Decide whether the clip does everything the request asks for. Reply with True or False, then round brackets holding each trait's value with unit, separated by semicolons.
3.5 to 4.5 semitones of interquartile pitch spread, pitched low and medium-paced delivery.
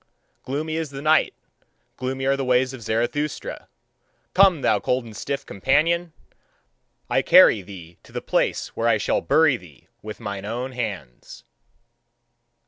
False (5.5 semitones; 130 Hz; 145 wpm)